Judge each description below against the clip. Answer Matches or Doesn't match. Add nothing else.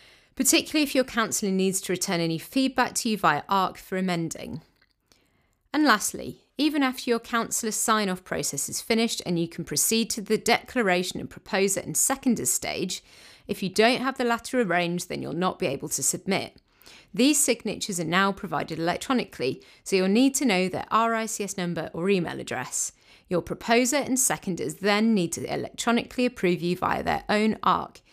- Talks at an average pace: Matches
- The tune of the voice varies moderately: Matches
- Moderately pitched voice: Doesn't match